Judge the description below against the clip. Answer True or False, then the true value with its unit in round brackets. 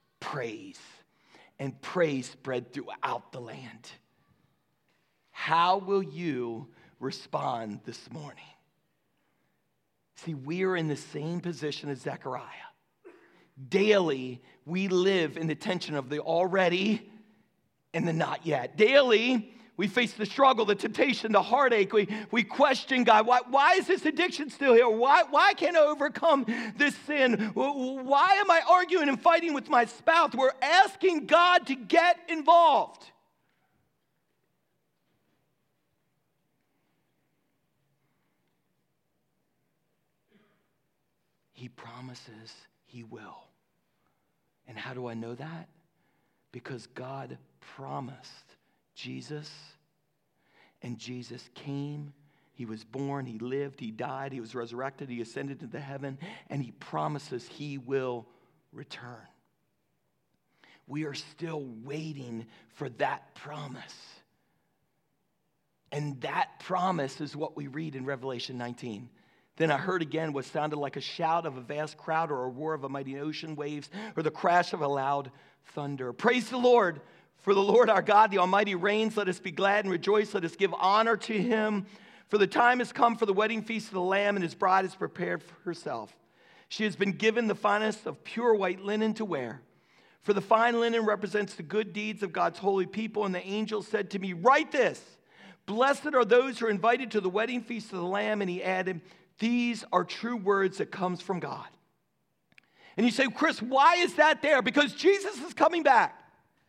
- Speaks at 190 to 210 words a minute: False (150 wpm)